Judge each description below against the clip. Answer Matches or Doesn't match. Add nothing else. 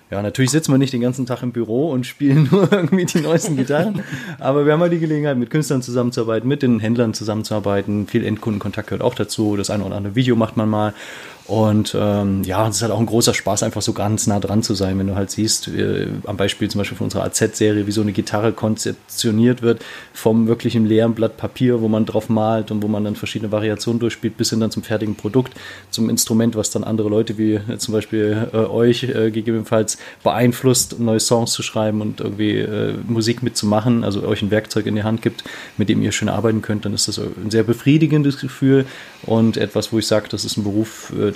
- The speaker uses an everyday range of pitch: Doesn't match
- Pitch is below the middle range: Matches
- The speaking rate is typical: Doesn't match